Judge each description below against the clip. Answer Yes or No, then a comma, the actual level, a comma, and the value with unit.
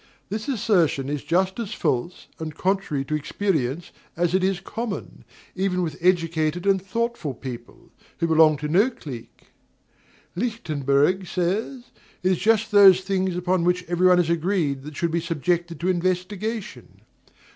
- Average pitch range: Yes, average, 3.5 semitones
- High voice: No, medium, 180 Hz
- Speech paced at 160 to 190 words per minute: No, average, 145 wpm